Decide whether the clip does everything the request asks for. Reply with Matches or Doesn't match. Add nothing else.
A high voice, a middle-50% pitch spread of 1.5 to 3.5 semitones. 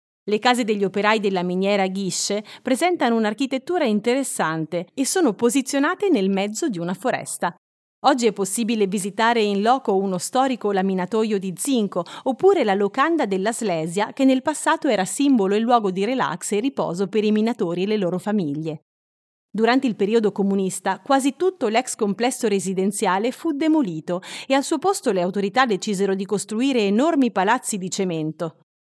Doesn't match